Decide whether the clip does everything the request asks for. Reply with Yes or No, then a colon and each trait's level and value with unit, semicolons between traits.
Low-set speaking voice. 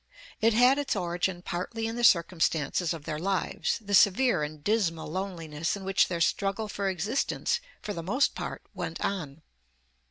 No: high, 190 Hz